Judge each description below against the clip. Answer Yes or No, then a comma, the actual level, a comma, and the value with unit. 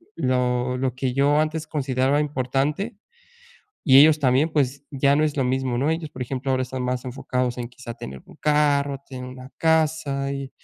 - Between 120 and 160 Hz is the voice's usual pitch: Yes, low, 135 Hz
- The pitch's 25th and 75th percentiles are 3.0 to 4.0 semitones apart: No, narrow, 2.6 semitones